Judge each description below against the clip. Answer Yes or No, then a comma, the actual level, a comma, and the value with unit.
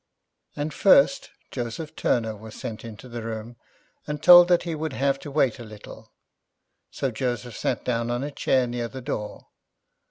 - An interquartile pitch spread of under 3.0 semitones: No, average, 4.3 semitones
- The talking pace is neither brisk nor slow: Yes, average, 170 wpm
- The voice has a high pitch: No, low, 125 Hz